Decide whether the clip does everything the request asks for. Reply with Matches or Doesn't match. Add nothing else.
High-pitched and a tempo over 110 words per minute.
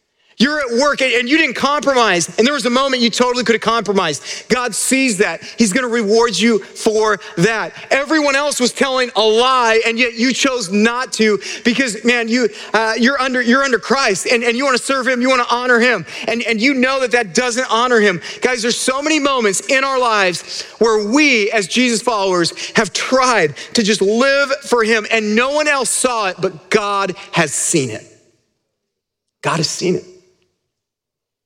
Matches